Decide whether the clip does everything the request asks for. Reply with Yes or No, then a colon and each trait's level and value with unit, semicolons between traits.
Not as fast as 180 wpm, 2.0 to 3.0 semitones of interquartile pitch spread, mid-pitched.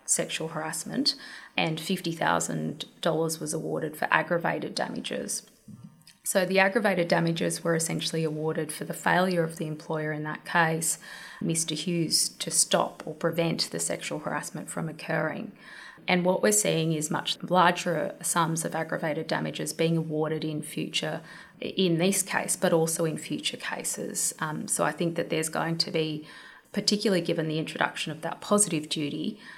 Yes: average, 155 wpm; narrow, 2.5 semitones; medium, 165 Hz